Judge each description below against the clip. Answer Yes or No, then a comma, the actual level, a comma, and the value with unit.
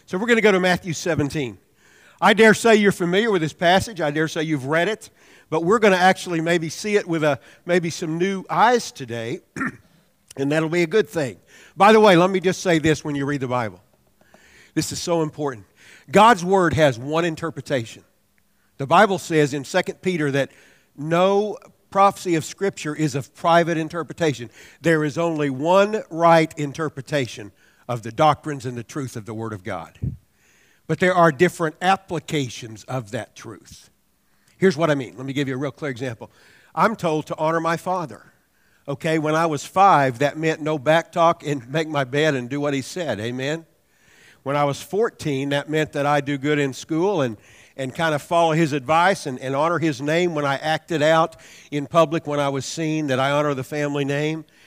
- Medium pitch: Yes, medium, 155 Hz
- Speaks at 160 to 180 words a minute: No, average, 200 wpm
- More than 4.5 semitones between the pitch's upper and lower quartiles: No, average, 3.5 semitones